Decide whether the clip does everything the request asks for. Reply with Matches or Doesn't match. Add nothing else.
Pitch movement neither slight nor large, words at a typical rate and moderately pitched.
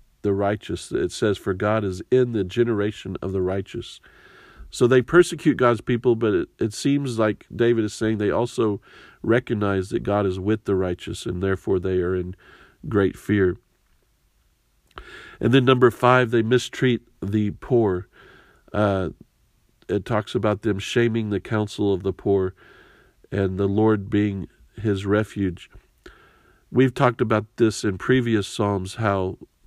Doesn't match